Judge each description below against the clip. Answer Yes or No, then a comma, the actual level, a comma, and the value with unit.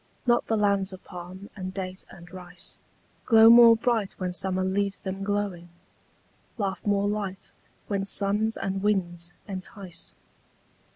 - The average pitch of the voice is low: No, high, 195 Hz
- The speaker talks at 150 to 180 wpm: No, slow, 135 wpm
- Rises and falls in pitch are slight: Yes, narrow, 1.8 semitones